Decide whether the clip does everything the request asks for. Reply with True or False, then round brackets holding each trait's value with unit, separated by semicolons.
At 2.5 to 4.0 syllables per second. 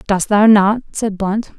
True (3.8 syllables/s)